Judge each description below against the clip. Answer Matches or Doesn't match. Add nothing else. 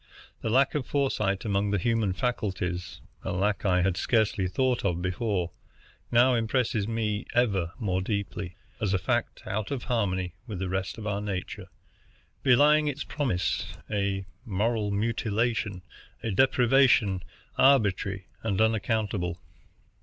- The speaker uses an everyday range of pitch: Matches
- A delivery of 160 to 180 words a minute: Doesn't match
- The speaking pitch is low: Matches